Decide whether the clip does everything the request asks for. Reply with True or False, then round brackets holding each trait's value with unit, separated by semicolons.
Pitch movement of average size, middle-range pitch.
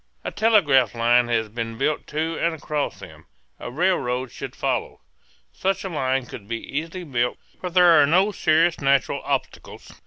False (5.7 semitones; 145 Hz)